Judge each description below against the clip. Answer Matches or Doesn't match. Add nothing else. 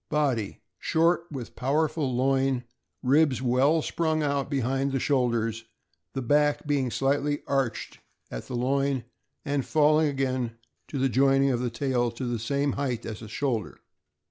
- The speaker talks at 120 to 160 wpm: Matches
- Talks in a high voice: Doesn't match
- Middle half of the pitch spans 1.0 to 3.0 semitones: Matches